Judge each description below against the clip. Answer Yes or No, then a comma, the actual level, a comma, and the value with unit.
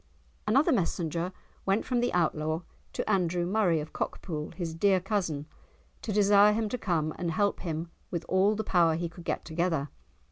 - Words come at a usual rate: Yes, average, 175 wpm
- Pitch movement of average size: Yes, average, 3.8 semitones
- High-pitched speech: No, medium, 180 Hz